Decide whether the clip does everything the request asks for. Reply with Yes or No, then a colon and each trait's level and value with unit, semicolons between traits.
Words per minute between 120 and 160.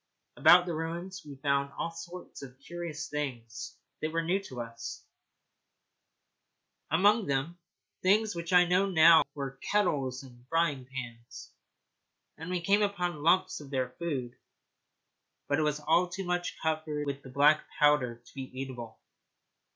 Yes: average, 150 wpm